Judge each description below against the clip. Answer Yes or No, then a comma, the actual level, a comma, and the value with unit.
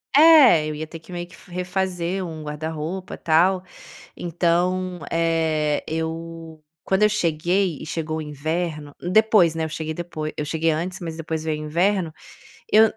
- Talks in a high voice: No, medium, 165 Hz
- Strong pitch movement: No, narrow, 2.5 semitones